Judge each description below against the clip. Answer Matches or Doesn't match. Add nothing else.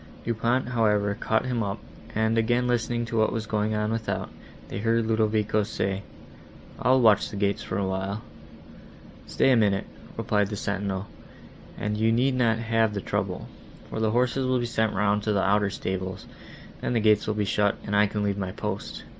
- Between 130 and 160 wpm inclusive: Doesn't match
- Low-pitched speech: Matches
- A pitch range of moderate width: Doesn't match